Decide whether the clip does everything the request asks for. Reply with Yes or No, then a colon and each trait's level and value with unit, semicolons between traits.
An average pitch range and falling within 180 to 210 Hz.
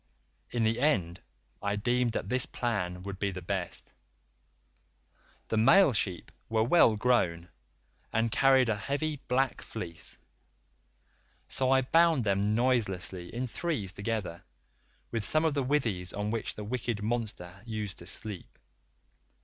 No: average, 4.5 semitones; low, 110 Hz